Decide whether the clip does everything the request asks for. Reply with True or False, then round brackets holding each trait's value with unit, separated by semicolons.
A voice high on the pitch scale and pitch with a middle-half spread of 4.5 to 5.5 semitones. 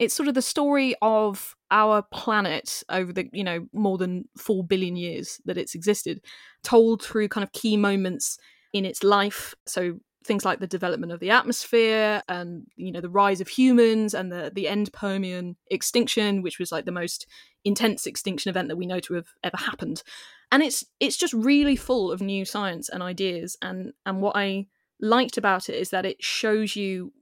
False (200 Hz; 3.4 semitones)